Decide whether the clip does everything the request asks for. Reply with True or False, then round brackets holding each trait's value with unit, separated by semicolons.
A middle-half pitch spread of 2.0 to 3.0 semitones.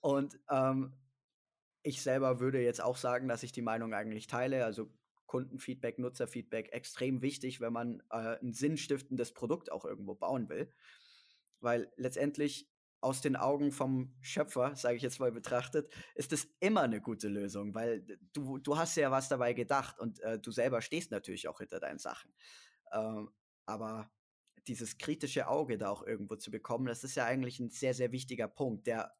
True (2.5 semitones)